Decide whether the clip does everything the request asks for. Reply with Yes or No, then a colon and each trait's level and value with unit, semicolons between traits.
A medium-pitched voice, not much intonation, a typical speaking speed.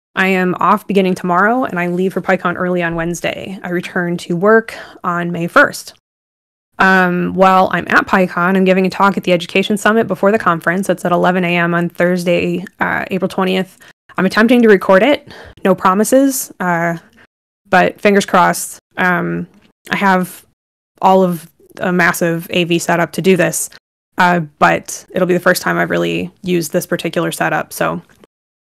Yes: medium, 180 Hz; narrow, 1.7 semitones; average, 170 wpm